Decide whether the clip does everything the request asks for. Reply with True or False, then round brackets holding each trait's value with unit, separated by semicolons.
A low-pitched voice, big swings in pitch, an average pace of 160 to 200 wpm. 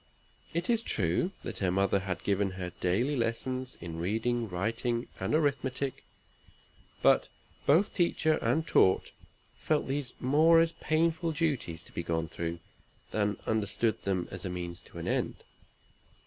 False (115 Hz; 7.8 semitones; 140 wpm)